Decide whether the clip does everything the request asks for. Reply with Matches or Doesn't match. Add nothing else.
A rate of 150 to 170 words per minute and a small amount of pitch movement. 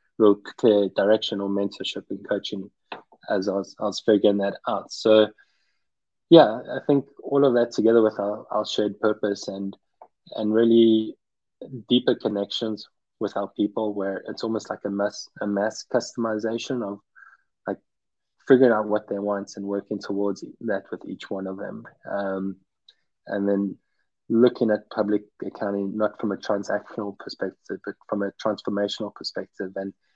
Matches